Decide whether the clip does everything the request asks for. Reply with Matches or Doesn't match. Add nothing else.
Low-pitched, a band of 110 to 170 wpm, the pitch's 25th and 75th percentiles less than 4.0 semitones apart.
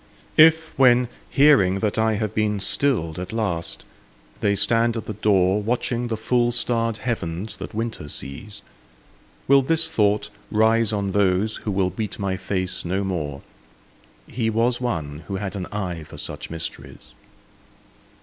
Matches